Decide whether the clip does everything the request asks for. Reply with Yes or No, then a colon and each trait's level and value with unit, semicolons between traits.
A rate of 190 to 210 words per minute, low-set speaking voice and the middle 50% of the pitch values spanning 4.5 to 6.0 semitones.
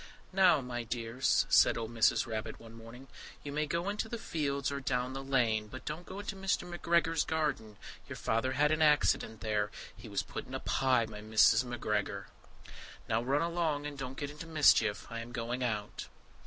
Yes: average, 195 wpm; low, 130 Hz; average, 5.1 semitones